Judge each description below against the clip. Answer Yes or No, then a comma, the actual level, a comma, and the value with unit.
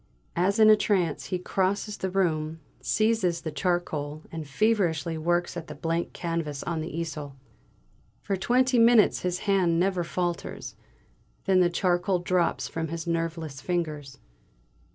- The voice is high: No, medium, 175 Hz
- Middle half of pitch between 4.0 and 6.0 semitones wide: No, average, 2.8 semitones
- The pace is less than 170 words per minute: Yes, average, 140 wpm